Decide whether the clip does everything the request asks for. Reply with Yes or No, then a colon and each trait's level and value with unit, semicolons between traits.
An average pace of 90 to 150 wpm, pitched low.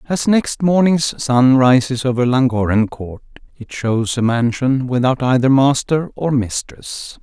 Yes: average, 140 wpm; low, 130 Hz